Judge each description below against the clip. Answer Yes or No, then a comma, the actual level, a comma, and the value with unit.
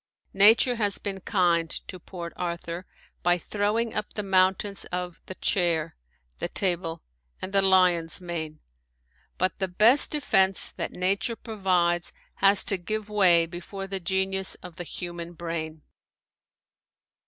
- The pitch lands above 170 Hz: Yes, medium, 185 Hz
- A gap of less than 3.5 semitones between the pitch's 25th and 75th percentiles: Yes, narrow, 2.4 semitones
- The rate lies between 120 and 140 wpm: Yes, slow, 135 wpm